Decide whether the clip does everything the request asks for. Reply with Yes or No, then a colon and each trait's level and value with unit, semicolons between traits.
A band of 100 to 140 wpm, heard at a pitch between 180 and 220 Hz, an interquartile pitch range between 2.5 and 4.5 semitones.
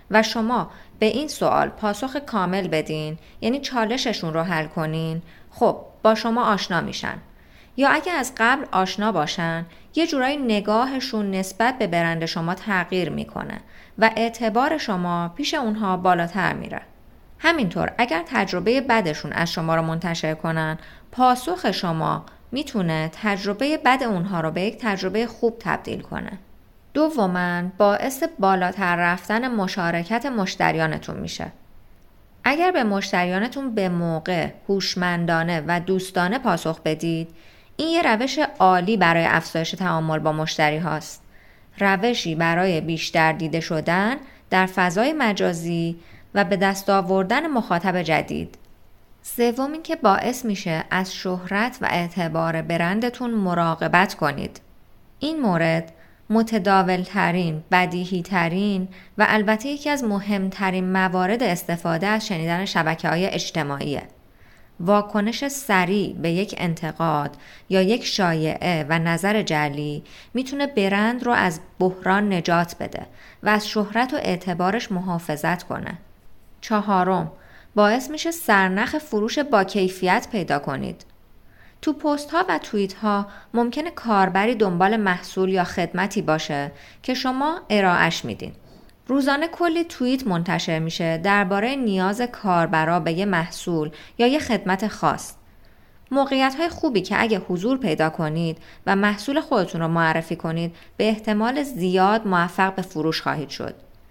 No: average, 125 wpm; high, 190 Hz; average, 5.2 semitones